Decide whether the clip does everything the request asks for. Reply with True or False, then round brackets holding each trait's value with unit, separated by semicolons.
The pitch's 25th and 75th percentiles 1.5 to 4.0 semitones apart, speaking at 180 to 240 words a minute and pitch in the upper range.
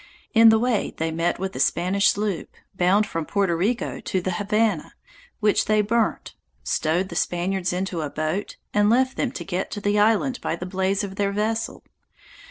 True (3.1 semitones; 185 wpm; 200 Hz)